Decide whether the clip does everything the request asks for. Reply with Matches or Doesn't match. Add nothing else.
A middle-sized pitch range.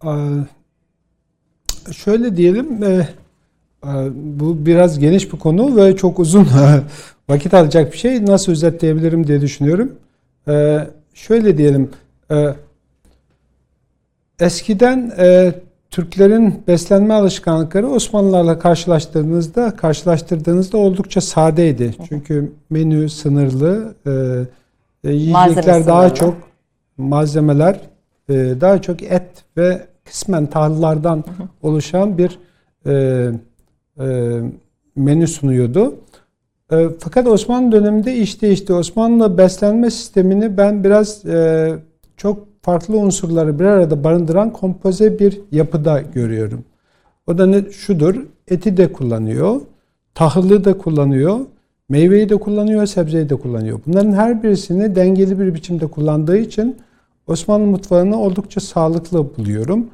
Matches